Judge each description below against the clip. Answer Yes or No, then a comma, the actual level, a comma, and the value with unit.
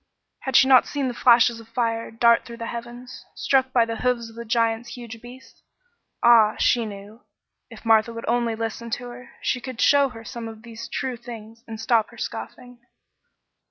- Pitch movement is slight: Yes, narrow, 1.4 semitones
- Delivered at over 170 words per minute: Yes, average, 195 wpm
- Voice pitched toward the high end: Yes, high, 235 Hz